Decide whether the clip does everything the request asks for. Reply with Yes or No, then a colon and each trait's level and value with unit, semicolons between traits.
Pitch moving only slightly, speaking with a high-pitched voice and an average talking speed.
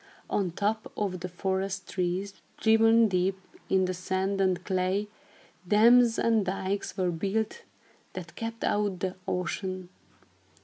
No: narrow, 2.3 semitones; high, 195 Hz; slow, 130 wpm